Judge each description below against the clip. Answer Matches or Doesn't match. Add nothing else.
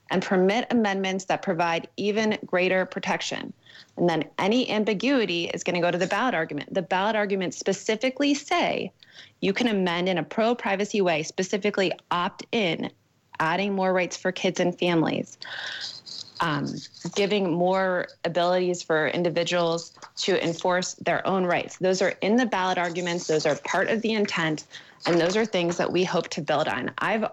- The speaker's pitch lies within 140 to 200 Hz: Matches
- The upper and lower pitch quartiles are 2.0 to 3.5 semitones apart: Matches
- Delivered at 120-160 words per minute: Doesn't match